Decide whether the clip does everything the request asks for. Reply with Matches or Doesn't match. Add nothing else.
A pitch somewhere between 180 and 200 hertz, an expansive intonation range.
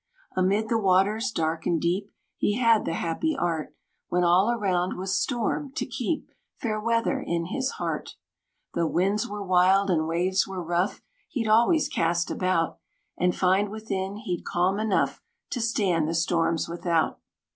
Doesn't match